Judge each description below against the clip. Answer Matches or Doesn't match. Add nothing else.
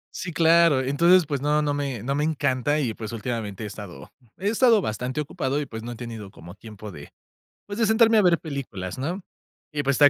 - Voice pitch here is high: Doesn't match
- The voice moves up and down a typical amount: Doesn't match